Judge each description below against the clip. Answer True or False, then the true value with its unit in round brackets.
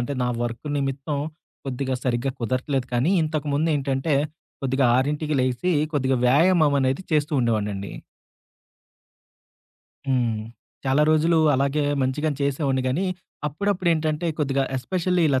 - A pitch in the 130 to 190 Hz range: True (140 Hz)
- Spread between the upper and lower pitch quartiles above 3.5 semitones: False (2.9 semitones)